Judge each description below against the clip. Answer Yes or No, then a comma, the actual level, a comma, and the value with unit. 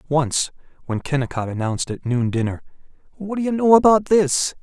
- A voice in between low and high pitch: Yes, medium, 155 Hz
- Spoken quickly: No, average, 170 wpm